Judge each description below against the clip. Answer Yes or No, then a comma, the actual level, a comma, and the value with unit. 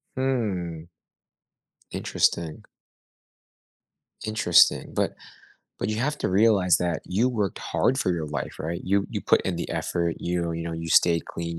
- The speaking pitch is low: Yes, very low, 90 Hz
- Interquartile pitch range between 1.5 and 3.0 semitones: No, average, 4.3 semitones